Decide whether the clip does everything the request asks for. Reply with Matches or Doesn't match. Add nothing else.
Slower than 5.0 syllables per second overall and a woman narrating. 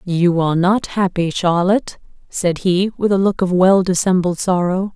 Matches